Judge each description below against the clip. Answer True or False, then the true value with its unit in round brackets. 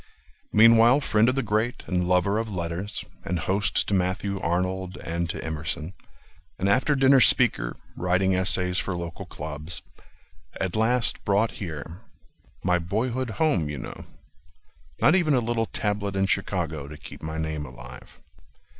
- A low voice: True (95 Hz)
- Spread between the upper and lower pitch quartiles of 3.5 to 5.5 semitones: True (4.9 semitones)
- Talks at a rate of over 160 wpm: False (150 wpm)